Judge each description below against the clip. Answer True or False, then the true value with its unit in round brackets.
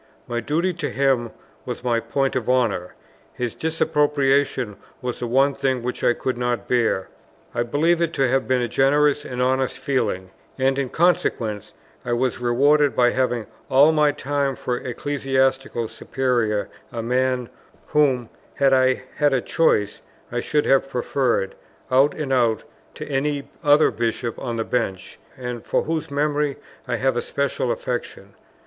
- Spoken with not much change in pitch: False (3.0 semitones)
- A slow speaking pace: False (160 wpm)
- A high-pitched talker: False (130 Hz)